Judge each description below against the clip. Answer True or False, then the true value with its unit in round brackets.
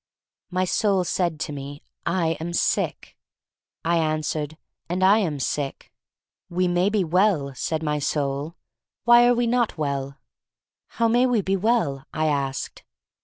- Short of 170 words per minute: True (150 wpm)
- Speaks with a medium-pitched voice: True (170 Hz)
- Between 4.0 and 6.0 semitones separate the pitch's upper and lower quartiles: True (5.1 semitones)